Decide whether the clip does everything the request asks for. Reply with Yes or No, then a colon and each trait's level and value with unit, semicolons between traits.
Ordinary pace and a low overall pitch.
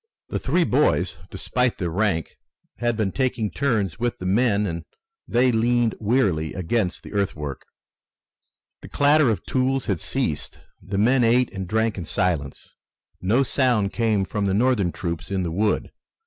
Yes: average, 160 wpm; low, 105 Hz